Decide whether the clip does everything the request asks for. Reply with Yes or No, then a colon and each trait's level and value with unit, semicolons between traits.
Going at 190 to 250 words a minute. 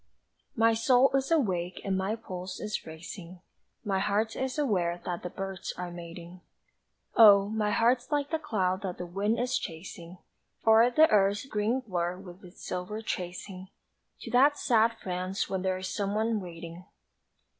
No: average, 155 wpm